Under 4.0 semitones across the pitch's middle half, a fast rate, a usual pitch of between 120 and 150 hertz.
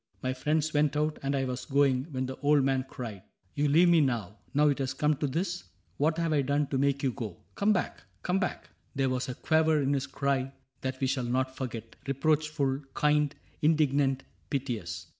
Yes: narrow, 2.4 semitones; fast, 215 wpm; medium, 140 Hz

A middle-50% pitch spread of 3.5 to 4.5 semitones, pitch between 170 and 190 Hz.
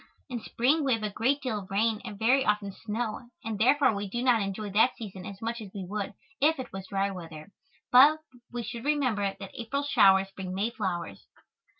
No: average, 4.0 semitones; high, 215 Hz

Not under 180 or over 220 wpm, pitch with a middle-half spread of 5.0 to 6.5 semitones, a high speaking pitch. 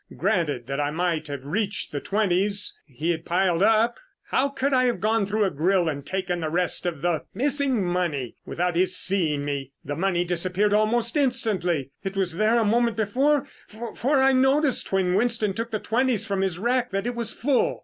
Yes: average, 195 wpm; average, 5.3 semitones; high, 195 Hz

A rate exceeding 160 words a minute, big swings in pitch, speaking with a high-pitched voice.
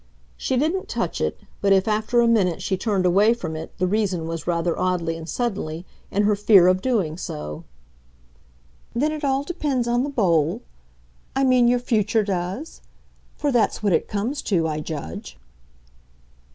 Yes: average, 170 wpm; wide, 5.9 semitones; high, 200 Hz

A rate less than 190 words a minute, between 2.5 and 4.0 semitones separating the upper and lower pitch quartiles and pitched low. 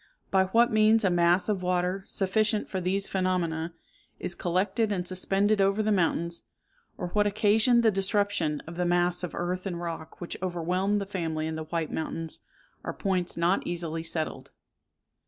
No: average, 170 wpm; average, 2.8 semitones; medium, 185 Hz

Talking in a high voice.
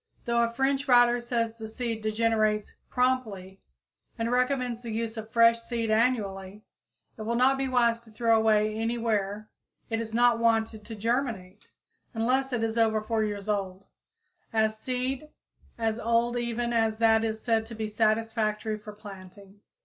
Yes: high, 225 Hz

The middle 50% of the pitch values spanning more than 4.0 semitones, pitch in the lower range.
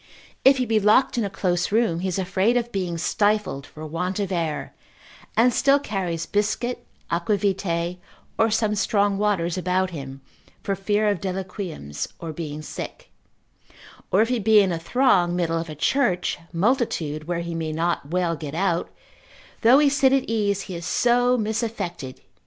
No: average, 4.4 semitones; high, 190 Hz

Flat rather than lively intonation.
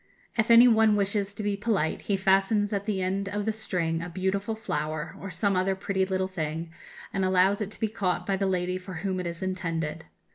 Yes: narrow, 2.1 semitones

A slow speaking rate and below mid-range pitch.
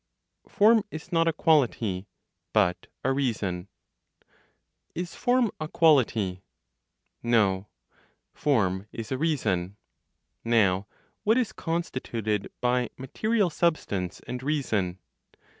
Yes: slow, 100 wpm; low, 125 Hz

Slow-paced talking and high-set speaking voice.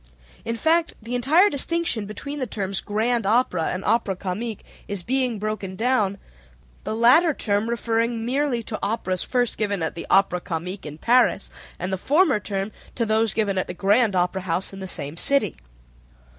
No: average, 175 wpm; high, 215 Hz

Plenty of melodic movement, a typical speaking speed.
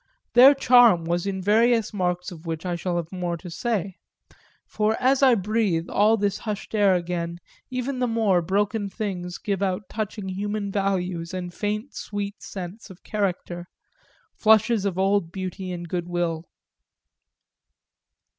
No: average, 3.4 semitones; average, 150 wpm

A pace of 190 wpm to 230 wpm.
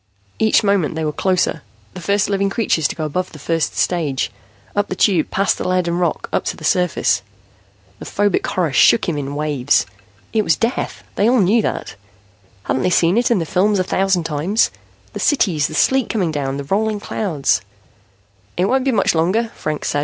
Yes: average, 200 wpm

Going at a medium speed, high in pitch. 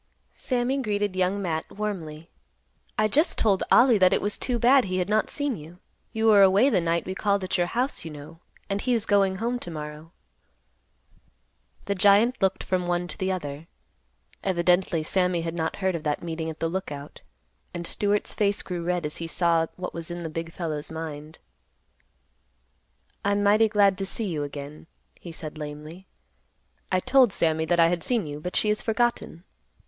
No: average, 190 wpm; medium, 180 Hz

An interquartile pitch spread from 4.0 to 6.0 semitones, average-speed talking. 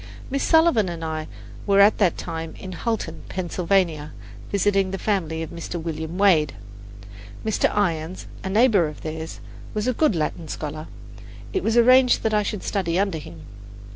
Yes: average, 4.5 semitones; average, 165 wpm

